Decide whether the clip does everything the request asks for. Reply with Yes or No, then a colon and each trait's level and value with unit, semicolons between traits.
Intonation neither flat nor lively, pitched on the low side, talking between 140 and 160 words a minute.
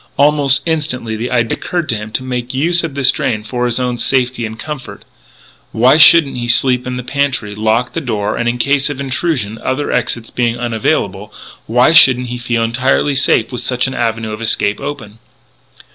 No: average, 3.1 semitones; low, 125 Hz; average, 190 wpm